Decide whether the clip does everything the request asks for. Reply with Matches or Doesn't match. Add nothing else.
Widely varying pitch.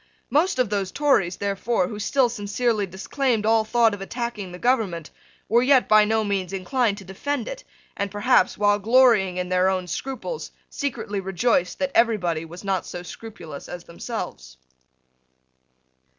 Doesn't match